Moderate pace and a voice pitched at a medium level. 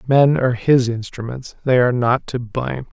No: average, 180 wpm; low, 125 Hz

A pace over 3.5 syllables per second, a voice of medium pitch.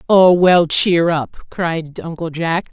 No: 3.2 syllables/s; medium, 170 Hz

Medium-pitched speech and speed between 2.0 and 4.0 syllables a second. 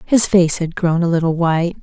No: medium, 170 Hz; 5.3 syllables/s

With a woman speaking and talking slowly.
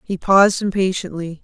Yes: female; slow, 125 wpm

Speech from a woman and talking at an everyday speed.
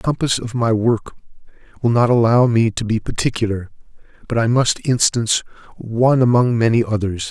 No: male; average, 165 wpm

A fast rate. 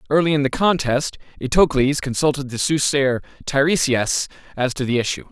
No: average, 145 wpm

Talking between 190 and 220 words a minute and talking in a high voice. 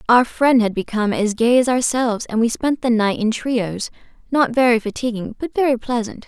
Yes: average, 200 wpm; high, 235 Hz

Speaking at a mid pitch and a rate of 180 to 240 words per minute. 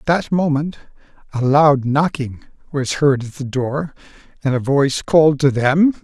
No: medium, 145 Hz; average, 170 wpm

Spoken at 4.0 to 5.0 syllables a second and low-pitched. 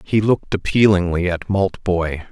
Yes: 4.6 syllables/s; very low, 95 Hz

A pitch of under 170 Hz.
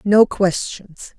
No: high, 195 Hz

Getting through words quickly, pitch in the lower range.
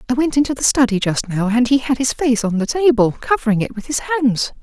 No: fast, 260 wpm; high, 245 Hz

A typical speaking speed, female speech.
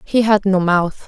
No: fast, 225 wpm; female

